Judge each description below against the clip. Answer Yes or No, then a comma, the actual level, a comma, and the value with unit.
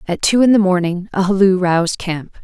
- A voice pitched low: No, high, 190 Hz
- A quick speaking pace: Yes, fast, 220 wpm